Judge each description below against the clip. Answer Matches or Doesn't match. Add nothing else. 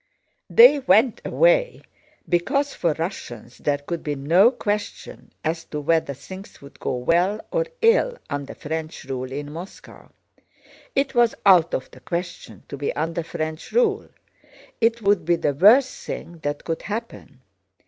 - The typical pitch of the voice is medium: Matches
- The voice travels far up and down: Matches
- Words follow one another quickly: Doesn't match